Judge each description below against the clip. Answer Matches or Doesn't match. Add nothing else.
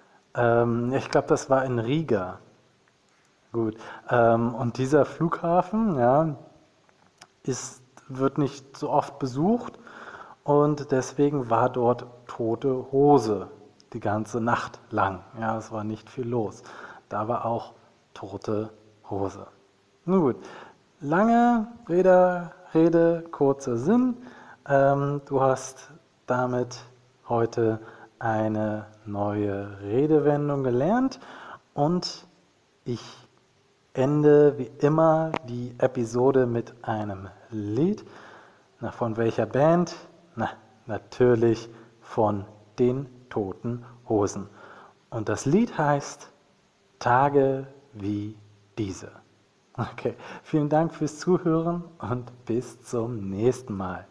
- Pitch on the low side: Matches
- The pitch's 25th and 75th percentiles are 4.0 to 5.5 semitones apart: Matches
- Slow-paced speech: Matches